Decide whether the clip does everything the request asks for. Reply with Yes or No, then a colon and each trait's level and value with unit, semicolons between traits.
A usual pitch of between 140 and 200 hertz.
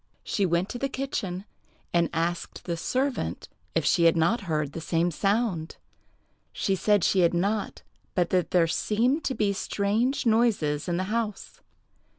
Yes: high, 190 Hz